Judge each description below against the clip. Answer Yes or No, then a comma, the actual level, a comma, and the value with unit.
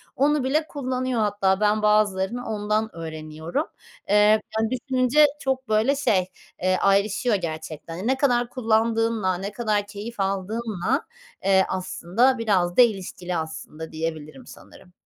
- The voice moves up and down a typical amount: Yes, average, 4.5 semitones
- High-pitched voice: Yes, high, 210 Hz